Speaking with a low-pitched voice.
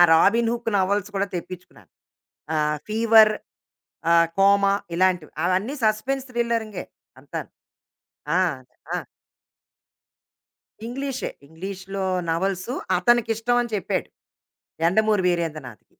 No: high, 200 Hz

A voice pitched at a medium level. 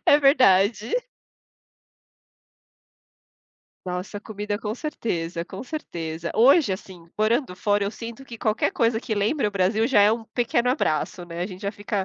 No: high, 210 Hz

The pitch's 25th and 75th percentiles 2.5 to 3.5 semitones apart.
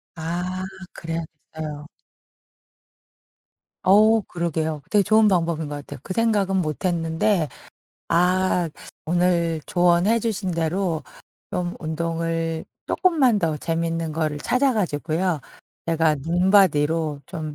Yes: average, 2.8 semitones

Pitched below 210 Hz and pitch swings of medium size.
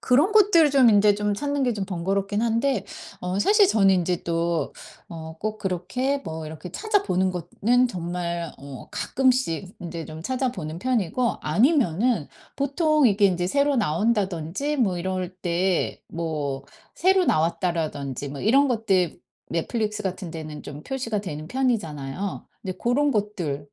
No: high, 195 Hz; wide, 7.0 semitones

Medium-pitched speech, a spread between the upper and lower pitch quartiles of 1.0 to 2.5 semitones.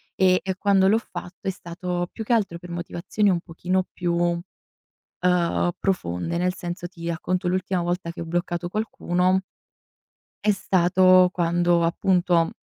Yes: medium, 180 Hz; narrow, 1.4 semitones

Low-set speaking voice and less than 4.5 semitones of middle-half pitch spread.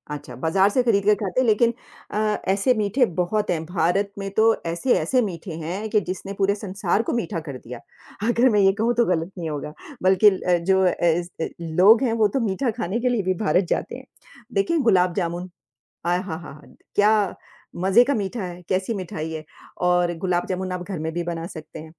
No: high, 190 Hz; average, 3.5 semitones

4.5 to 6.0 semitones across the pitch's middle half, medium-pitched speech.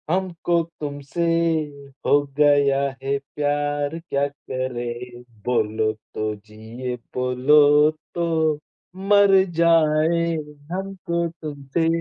Yes: average, 4.8 semitones; medium, 145 Hz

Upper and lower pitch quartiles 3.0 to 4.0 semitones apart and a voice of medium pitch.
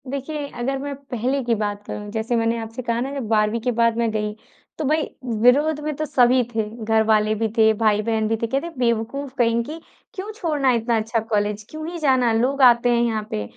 No: average, 3.7 semitones; high, 235 Hz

